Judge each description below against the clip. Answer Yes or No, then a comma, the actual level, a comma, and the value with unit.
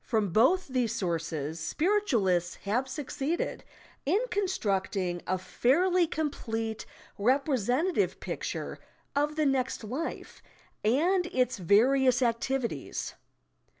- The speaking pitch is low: No, very high, 255 Hz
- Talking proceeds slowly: Yes, slow, 95 wpm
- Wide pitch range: Yes, wide, 6.8 semitones